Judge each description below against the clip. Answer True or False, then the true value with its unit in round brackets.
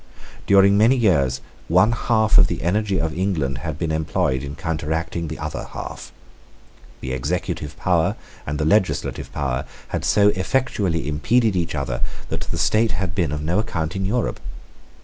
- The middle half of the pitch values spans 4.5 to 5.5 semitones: True (4.9 semitones)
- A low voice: True (85 Hz)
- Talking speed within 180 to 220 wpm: False (165 wpm)